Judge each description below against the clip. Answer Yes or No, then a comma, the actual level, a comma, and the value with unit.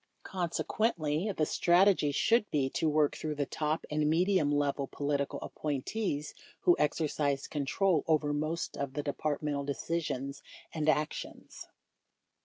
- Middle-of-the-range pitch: Yes, medium, 150 Hz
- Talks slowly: Yes, slow, 125 wpm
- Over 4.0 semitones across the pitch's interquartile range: No, narrow, 2.6 semitones